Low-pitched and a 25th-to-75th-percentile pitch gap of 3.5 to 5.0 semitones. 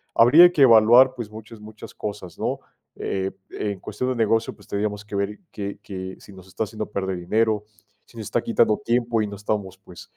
No: low, 105 Hz; narrow, 2.4 semitones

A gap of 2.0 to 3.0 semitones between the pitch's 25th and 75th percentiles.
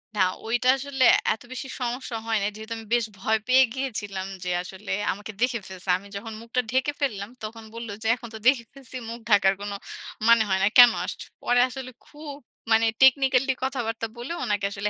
No: average, 3.7 semitones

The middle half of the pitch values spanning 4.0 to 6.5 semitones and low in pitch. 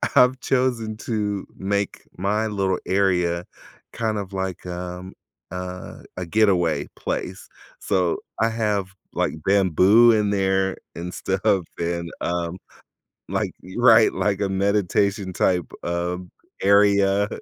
No: narrow, 2.5 semitones; very low, 95 Hz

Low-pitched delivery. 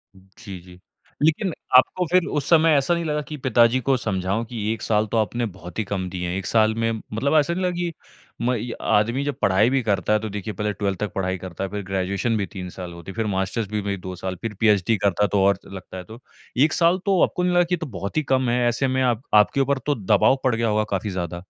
Yes: low, 110 Hz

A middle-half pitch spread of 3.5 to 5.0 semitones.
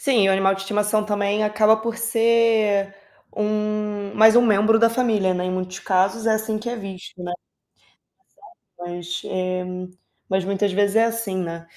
No: narrow, 2.6 semitones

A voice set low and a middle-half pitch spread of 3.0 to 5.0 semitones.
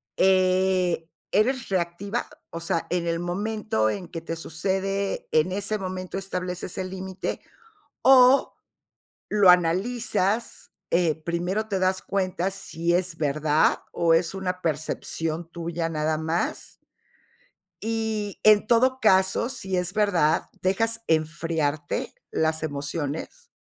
No: medium, 185 Hz; average, 3.4 semitones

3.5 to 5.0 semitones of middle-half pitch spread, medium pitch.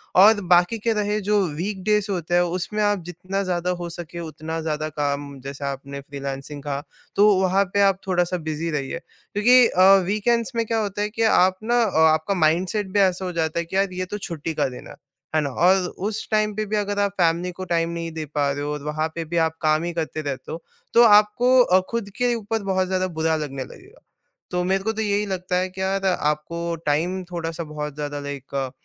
Yes: average, 4.6 semitones; medium, 180 Hz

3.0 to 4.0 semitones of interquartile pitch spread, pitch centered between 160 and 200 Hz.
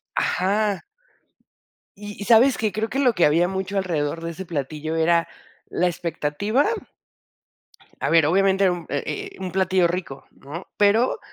Yes: average, 3.5 semitones; medium, 185 Hz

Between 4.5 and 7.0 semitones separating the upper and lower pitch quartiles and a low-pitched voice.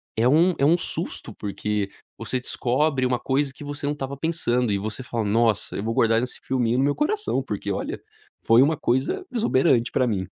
No: average, 4.1 semitones; low, 130 Hz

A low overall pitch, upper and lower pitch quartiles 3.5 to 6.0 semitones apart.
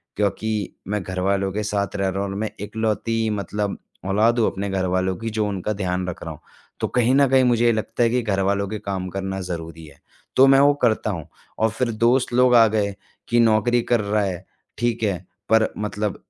No: low, 105 Hz; average, 2.9 semitones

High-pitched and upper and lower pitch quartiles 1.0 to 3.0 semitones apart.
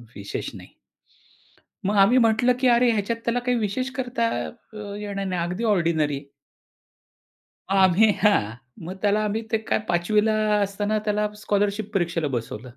No: high, 205 Hz; average, 3.5 semitones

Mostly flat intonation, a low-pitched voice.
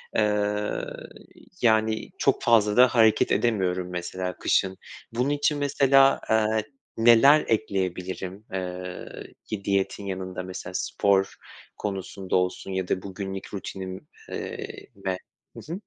No: average, 3.7 semitones; low, 100 Hz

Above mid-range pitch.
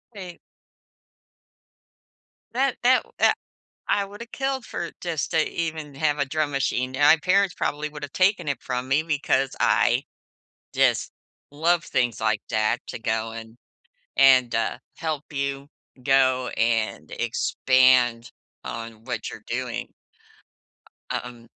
No: medium, 140 Hz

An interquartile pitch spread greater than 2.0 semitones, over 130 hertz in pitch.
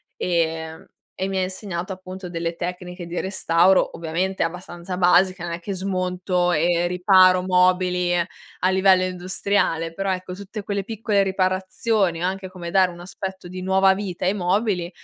No: narrow, 1.4 semitones; medium, 185 Hz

